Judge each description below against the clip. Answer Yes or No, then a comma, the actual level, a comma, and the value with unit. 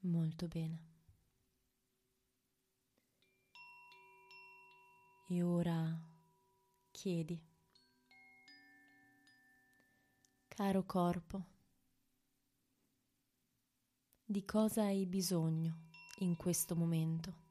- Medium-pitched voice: Yes, medium, 165 Hz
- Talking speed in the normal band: No, slow, 50 wpm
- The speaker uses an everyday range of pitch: No, wide, 7.2 semitones